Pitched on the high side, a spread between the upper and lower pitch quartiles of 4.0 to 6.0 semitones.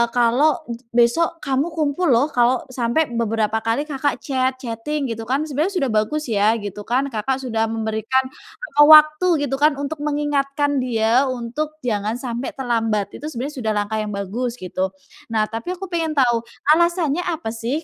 Yes: very high, 255 Hz; average, 4.5 semitones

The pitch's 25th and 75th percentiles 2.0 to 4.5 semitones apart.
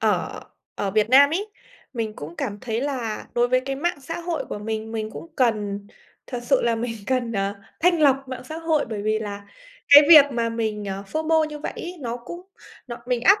No: average, 5.2 semitones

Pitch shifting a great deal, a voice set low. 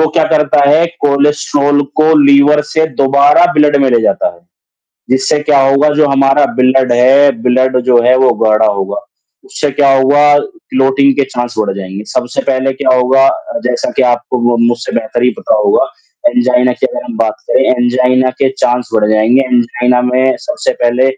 No: average, 2.9 semitones; low, 130 Hz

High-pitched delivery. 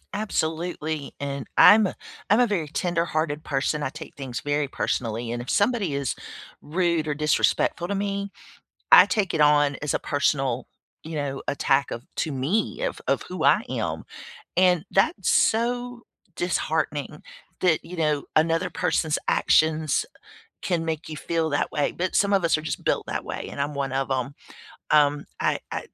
No: medium, 155 Hz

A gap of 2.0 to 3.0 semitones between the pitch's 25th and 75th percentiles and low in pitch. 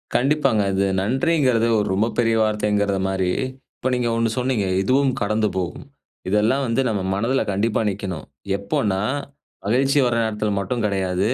No: average, 3.7 semitones; low, 110 Hz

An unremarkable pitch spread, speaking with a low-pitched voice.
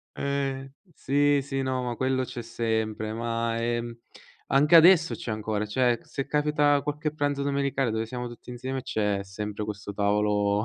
Yes: average, 4.4 semitones; low, 125 Hz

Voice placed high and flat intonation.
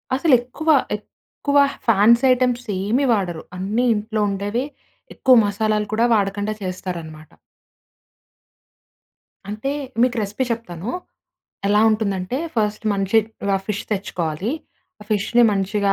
No: high, 210 Hz; average, 3.2 semitones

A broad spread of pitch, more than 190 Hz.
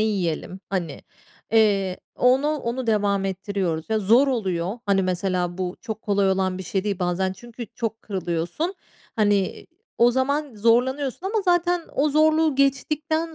Yes: wide, 6.3 semitones; high, 215 Hz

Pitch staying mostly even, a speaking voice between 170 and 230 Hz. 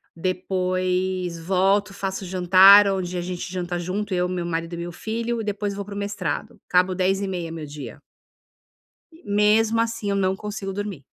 Yes: narrow, 2.2 semitones; high, 190 Hz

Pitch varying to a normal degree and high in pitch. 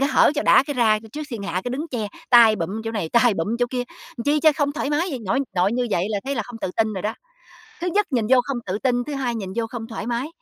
Yes: average, 4.4 semitones; high, 240 Hz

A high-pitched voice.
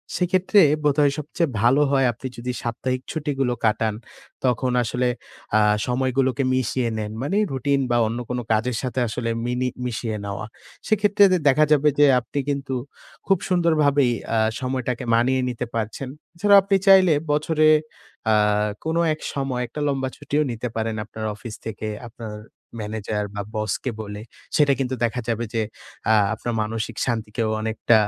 No: low, 125 Hz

